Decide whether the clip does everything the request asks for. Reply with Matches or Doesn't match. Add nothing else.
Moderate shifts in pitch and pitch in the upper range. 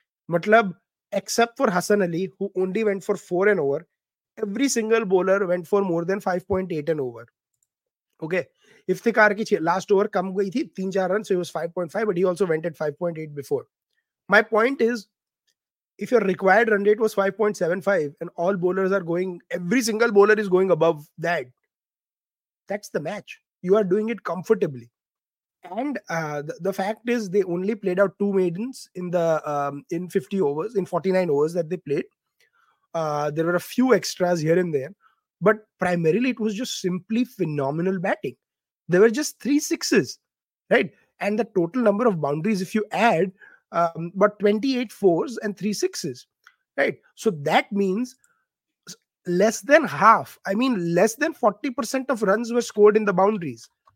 Matches